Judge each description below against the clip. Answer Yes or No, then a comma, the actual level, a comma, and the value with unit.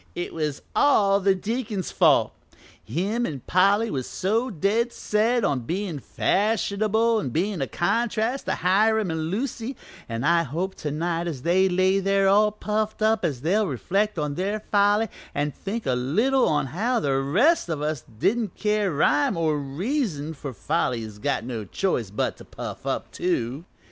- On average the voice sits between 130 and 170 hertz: No, medium, 185 Hz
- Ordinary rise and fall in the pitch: No, wide, 6.4 semitones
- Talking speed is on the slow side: No, average, 175 wpm